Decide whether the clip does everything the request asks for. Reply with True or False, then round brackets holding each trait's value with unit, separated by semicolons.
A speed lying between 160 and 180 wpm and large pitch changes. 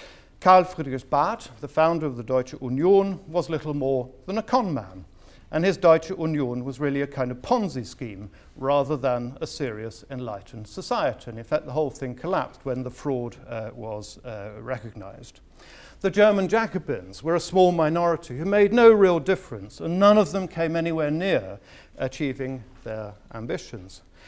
True (170 wpm; 6.1 semitones)